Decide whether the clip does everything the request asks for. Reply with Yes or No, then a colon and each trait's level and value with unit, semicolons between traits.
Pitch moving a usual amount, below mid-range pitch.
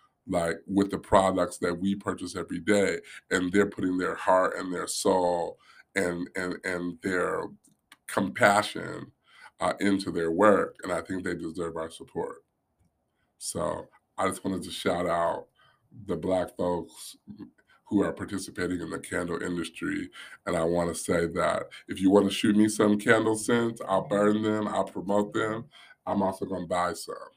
Yes: average, 3.0 semitones; very low, 95 Hz